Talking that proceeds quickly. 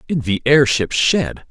No: average, 160 wpm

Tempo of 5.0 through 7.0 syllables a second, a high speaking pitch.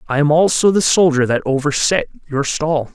No: 5.3 syllables/s; medium, 150 Hz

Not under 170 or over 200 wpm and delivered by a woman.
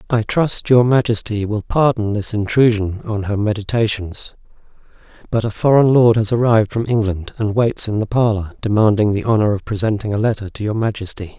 No: average, 180 wpm; male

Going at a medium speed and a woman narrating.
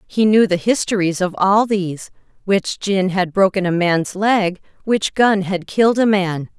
Yes: average, 175 wpm; female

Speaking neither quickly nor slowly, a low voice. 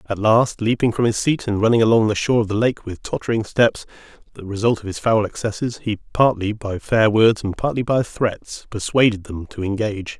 No: fast, 210 wpm; low, 110 Hz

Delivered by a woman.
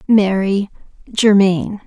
Yes: female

